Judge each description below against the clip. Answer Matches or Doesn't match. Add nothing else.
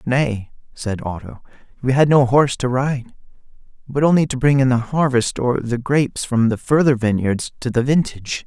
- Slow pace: Doesn't match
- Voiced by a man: Matches